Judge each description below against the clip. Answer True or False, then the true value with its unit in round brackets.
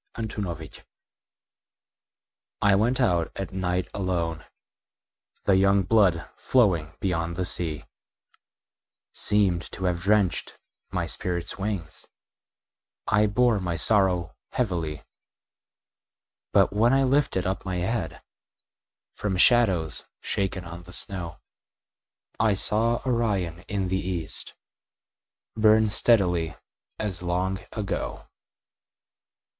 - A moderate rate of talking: False (105 wpm)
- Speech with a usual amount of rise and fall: True (3.5 semitones)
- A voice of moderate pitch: False (95 Hz)